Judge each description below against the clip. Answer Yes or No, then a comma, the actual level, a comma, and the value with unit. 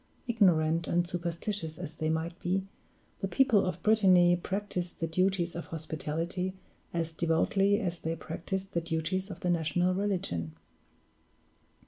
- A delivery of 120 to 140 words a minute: Yes, slow, 135 wpm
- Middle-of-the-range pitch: Yes, medium, 175 Hz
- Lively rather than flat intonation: No, average, 2.7 semitones